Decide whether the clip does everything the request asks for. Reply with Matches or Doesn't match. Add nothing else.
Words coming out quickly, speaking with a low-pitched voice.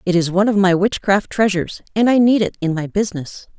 Doesn't match